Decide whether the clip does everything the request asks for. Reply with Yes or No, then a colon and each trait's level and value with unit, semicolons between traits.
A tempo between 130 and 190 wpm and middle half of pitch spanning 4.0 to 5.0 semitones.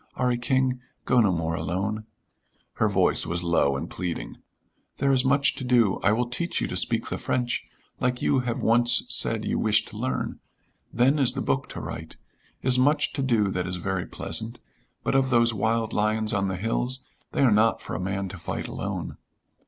No: average, 200 wpm; average, 4.7 semitones